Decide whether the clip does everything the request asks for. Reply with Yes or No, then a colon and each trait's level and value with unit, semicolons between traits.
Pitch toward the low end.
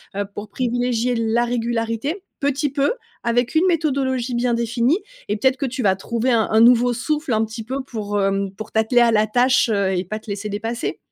No: high, 235 Hz